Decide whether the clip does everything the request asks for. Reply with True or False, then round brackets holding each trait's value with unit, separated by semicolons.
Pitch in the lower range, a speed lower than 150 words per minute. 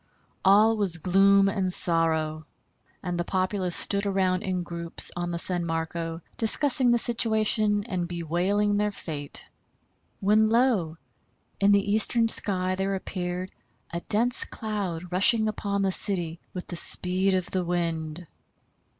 False (185 Hz; 140 wpm)